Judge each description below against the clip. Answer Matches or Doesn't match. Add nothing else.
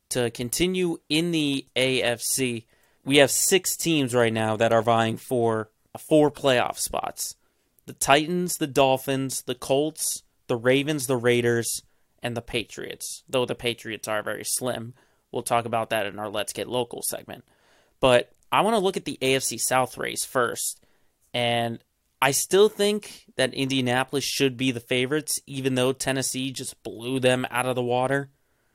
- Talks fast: Doesn't match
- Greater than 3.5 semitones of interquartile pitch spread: Doesn't match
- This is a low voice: Matches